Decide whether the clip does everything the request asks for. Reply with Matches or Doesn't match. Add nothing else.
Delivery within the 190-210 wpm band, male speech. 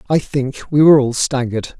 Matches